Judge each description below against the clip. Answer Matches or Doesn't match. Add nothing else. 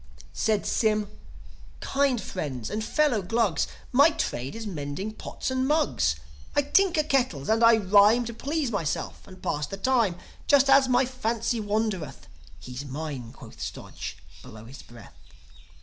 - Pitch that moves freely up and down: Matches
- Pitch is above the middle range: Matches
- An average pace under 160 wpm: Matches